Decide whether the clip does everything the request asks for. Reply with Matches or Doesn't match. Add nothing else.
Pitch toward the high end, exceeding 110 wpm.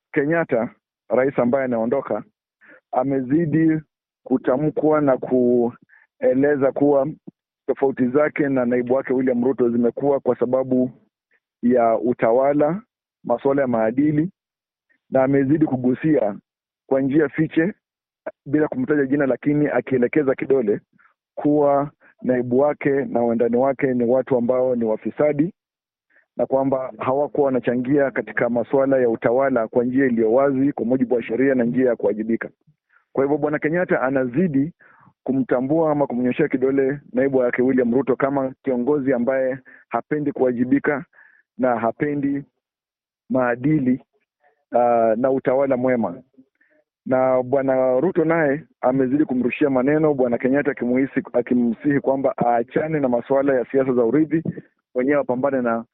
Doesn't match